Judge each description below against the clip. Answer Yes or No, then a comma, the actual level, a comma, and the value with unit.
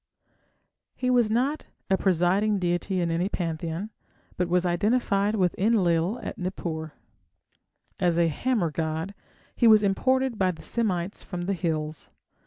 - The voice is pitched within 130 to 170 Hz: No, medium, 185 Hz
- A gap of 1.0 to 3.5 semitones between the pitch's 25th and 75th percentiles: No, average, 4.0 semitones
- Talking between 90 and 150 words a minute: Yes, average, 140 wpm